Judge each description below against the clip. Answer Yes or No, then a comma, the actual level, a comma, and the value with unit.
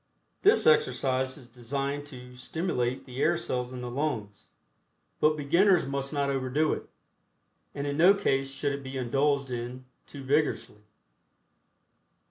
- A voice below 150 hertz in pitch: Yes, low, 135 Hz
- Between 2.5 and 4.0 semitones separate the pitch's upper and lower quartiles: Yes, average, 2.8 semitones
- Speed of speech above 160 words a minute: No, average, 140 wpm